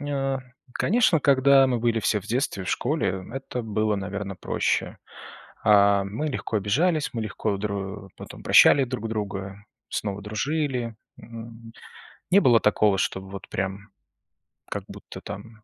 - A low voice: Yes, low, 110 Hz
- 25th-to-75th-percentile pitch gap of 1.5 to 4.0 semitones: No, average, 4.6 semitones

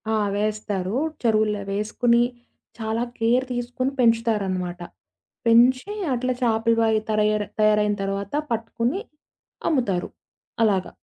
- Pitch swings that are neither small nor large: No, narrow, 2.3 semitones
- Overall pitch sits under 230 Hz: Yes, high, 220 Hz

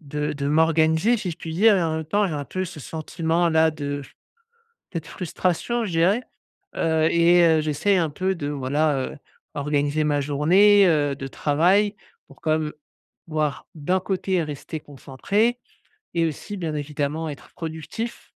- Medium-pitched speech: Yes, medium, 160 Hz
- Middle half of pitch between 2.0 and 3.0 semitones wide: No, average, 3.5 semitones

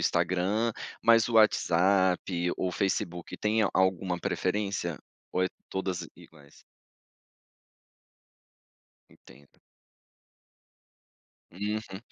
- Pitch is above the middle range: No, very low, 95 Hz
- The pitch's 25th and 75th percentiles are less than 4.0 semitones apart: Yes, average, 2.9 semitones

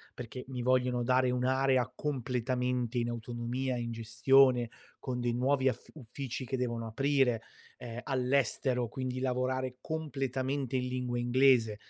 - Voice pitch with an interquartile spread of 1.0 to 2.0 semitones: Yes, narrow, 1.5 semitones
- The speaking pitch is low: Yes, low, 125 Hz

